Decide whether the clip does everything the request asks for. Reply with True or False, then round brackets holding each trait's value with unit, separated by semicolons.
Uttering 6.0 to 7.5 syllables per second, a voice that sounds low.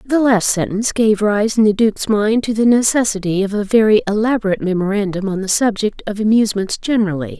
False (6.1 syllables/s; 210 Hz)